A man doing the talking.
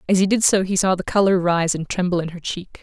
No: female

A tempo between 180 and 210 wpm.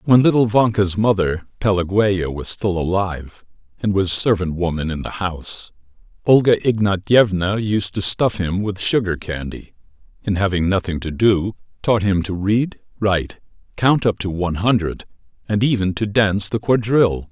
No: average, 155 wpm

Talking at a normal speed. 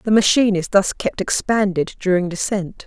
Yes: average, 165 wpm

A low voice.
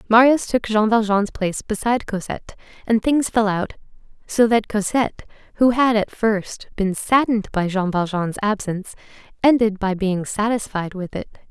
No: high, 210 Hz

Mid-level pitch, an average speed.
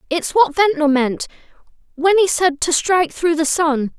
No: very high, 320 Hz; average, 180 wpm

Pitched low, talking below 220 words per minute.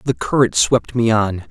Yes: low, 115 Hz; average, 200 wpm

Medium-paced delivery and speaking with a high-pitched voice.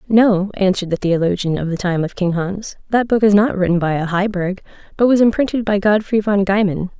No: fast, 215 wpm; high, 195 Hz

